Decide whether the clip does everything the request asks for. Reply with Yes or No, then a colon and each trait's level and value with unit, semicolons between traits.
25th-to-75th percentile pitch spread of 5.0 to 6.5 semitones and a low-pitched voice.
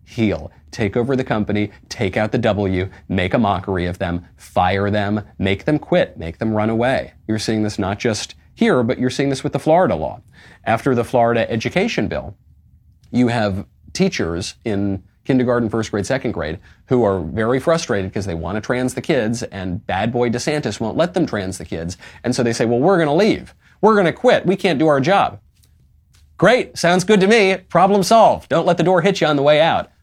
Yes: wide, 5.4 semitones; low, 115 Hz